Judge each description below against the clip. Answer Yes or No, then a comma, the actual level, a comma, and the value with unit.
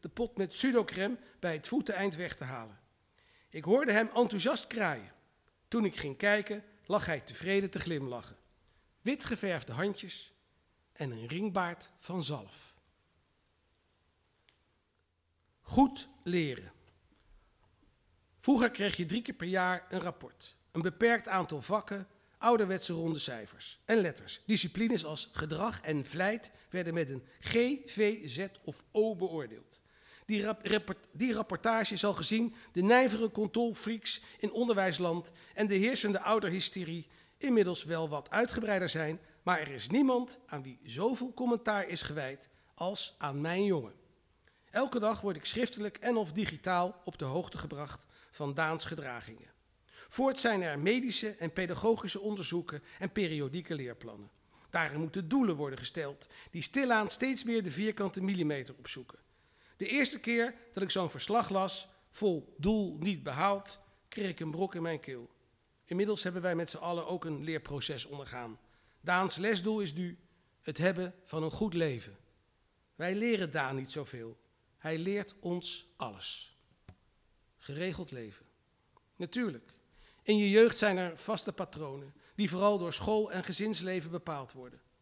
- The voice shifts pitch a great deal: Yes, wide, 6.3 semitones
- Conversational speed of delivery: Yes, average, 145 wpm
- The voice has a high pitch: No, medium, 180 Hz